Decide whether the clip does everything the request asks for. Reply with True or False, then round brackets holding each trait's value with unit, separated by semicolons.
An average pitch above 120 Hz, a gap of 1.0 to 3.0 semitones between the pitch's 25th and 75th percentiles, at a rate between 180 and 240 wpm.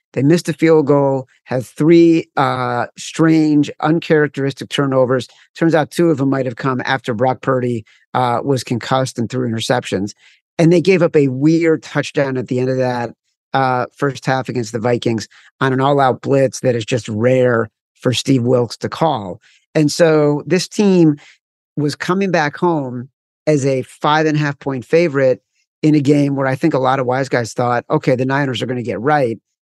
False (135 Hz; 3.4 semitones; 195 wpm)